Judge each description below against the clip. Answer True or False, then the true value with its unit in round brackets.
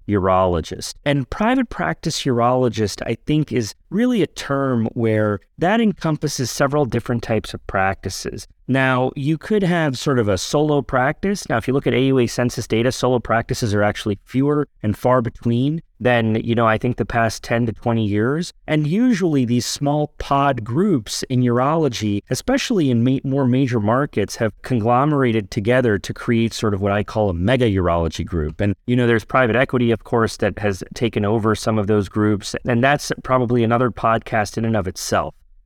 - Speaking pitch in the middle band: False (120 Hz)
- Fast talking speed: False (180 wpm)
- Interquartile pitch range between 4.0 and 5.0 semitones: True (4.3 semitones)